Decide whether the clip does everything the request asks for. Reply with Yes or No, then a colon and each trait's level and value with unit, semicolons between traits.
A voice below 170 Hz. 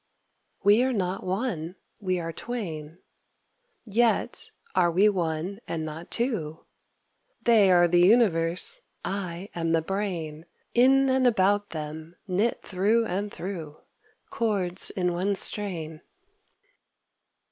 No: medium, 185 Hz